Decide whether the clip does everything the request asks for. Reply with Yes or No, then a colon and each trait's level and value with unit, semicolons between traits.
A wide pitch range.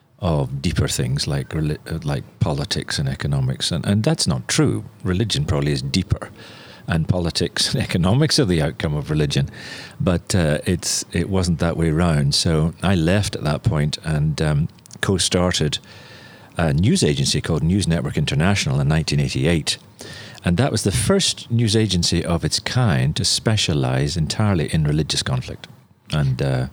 Yes: wide, 6.5 semitones